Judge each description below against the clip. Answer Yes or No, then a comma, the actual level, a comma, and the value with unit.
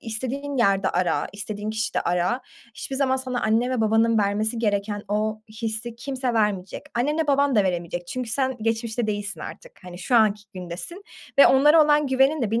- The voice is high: Yes, high, 225 Hz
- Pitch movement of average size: Yes, average, 4.2 semitones